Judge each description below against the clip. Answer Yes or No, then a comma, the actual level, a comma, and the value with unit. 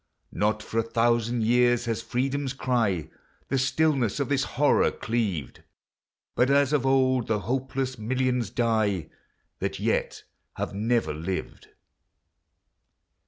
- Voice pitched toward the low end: Yes, low, 120 Hz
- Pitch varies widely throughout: No, average, 3.1 semitones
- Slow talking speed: Yes, slow, 120 wpm